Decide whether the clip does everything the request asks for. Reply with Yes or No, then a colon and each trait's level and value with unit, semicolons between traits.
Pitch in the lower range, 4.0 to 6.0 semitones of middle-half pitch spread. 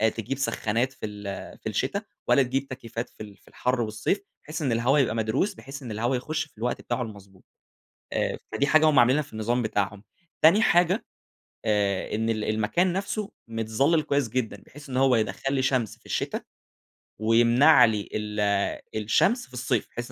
Yes: low, 120 Hz; average, 4.6 semitones